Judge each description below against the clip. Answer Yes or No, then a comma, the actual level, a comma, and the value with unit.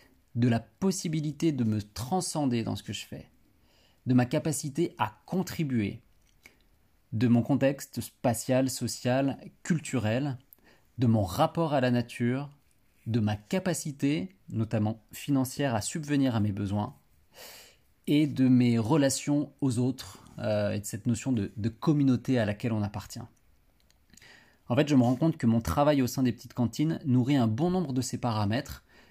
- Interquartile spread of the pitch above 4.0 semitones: Yes, average, 4.5 semitones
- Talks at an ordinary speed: Yes, average, 160 wpm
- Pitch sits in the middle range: No, low, 125 Hz